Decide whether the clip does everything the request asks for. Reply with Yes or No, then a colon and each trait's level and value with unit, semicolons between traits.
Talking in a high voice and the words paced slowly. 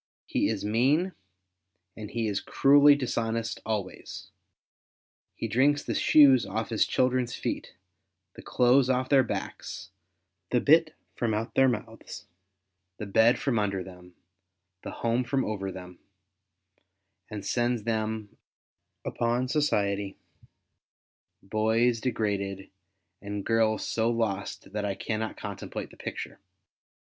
No: low, 115 Hz; slow, 120 wpm